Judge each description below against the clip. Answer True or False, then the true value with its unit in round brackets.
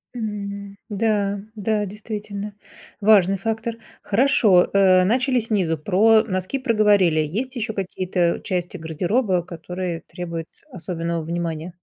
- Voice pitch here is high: True (195 Hz)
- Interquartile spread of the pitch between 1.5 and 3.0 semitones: False (3.5 semitones)